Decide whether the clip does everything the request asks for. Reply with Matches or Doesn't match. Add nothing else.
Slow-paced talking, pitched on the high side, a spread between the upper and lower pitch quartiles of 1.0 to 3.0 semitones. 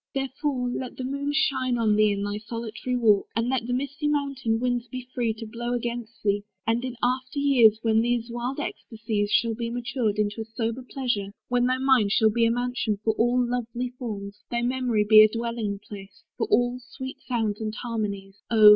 Doesn't match